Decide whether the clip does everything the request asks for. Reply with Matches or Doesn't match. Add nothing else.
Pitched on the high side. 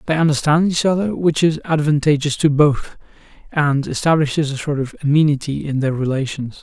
Doesn't match